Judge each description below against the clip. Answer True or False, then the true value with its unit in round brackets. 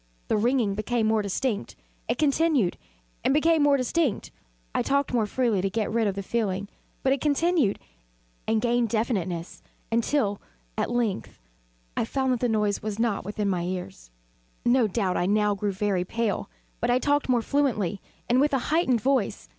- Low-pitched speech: False (225 Hz)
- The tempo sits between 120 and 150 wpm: False (175 wpm)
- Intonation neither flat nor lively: True (4.6 semitones)